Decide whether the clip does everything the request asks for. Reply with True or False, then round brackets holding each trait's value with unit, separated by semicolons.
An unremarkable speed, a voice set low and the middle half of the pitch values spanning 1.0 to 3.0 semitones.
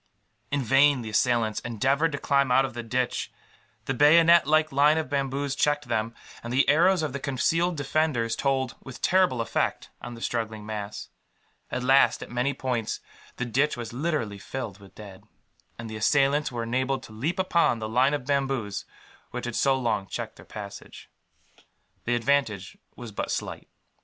False (175 wpm; 130 Hz; 3.7 semitones)